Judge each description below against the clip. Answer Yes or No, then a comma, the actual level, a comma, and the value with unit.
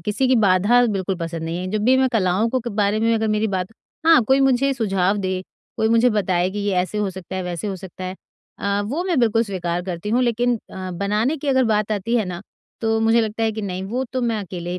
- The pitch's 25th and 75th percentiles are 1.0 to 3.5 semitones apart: No, average, 3.9 semitones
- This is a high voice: Yes, high, 210 Hz